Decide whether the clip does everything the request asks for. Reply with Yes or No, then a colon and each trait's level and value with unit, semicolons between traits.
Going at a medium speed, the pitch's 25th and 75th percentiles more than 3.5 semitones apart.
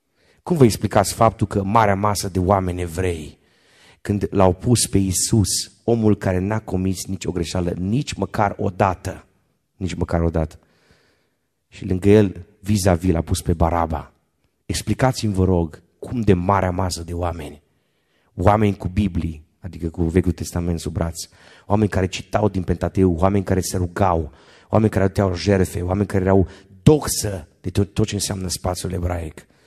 No: average, 160 wpm; average, 2.7 semitones